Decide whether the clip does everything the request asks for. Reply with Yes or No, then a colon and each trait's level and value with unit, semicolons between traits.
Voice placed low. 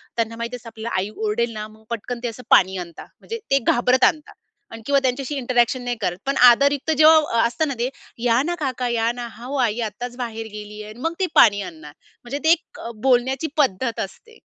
No: high, 240 Hz